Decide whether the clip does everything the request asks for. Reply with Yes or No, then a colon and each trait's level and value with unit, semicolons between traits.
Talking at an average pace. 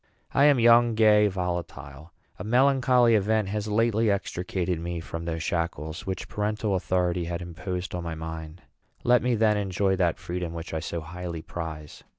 Yes: average, 165 wpm